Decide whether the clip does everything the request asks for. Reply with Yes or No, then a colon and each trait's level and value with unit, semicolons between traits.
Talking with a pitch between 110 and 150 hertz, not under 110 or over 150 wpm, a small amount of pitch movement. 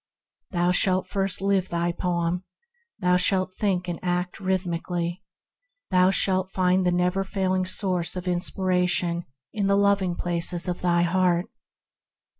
No: medium, 180 Hz; slow, 135 wpm; narrow, 1.2 semitones